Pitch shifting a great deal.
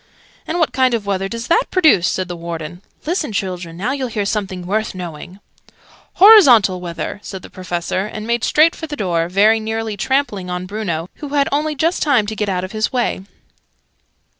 Yes: wide, 6.4 semitones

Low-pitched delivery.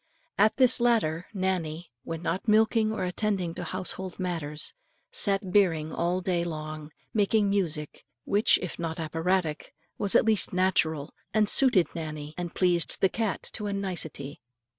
No: medium, 180 Hz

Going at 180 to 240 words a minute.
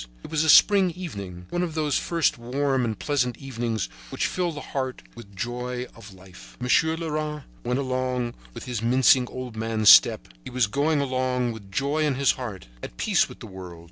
Yes: average, 200 wpm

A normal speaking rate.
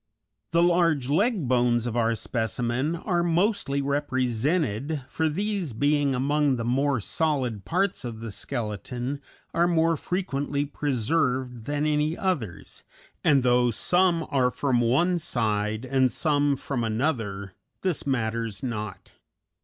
No: slow, 130 wpm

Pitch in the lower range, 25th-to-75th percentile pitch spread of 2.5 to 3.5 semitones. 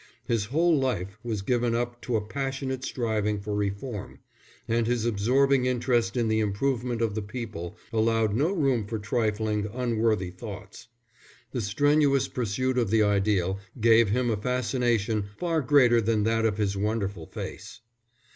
Yes: low, 115 Hz; average, 3.2 semitones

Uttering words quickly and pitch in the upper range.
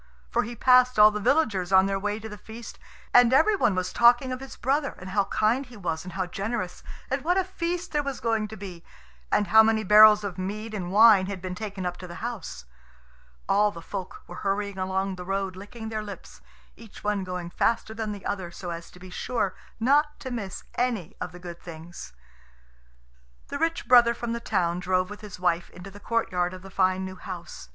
Yes: fast, 220 wpm; high, 205 Hz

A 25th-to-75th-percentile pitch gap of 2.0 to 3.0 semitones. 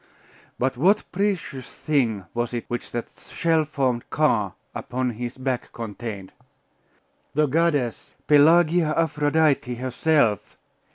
No: average, 4.6 semitones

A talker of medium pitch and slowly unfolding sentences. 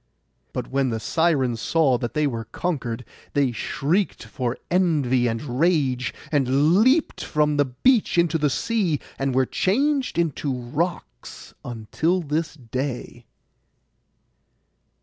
Yes: medium, 145 Hz; slow, 125 wpm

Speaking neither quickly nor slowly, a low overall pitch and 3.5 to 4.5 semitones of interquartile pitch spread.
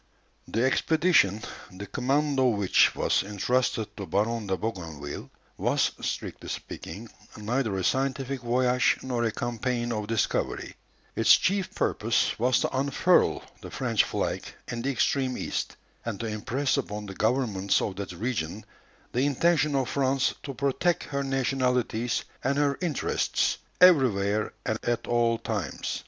Yes: average, 145 wpm; low, 120 Hz; average, 4.2 semitones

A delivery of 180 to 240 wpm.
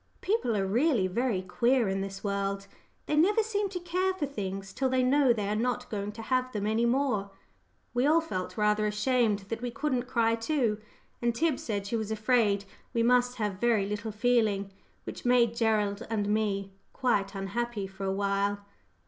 Yes: average, 185 wpm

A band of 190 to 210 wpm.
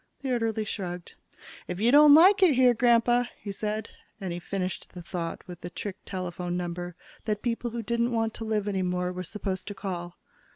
Yes: fast, 205 wpm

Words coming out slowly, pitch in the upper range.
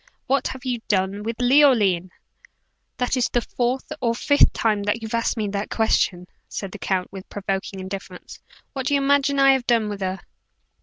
No: average, 190 wpm; high, 225 Hz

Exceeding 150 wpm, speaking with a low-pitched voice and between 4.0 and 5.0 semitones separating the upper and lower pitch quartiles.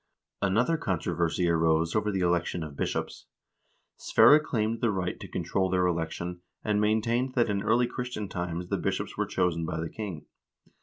Yes: average, 165 wpm; very low, 95 Hz; average, 4.4 semitones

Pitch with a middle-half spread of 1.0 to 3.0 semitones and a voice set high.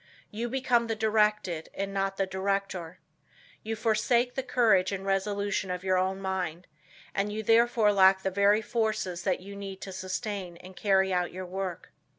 Yes: narrow, 2.4 semitones; high, 195 Hz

